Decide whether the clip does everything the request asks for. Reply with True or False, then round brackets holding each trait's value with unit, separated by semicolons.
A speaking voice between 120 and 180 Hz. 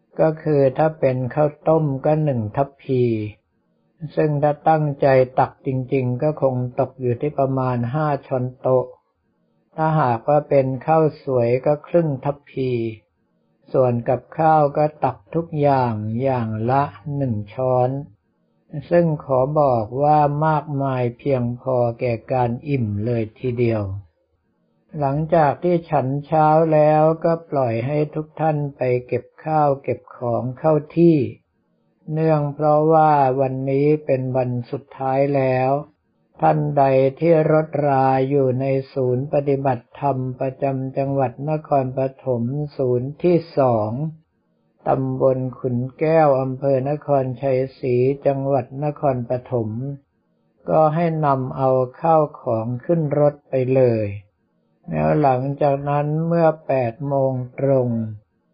True (135 Hz)